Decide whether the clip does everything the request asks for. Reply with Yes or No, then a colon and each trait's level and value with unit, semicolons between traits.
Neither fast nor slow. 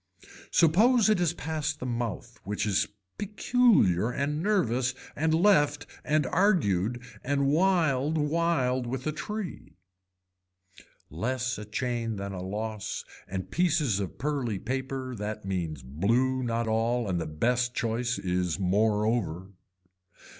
No: slow, 125 wpm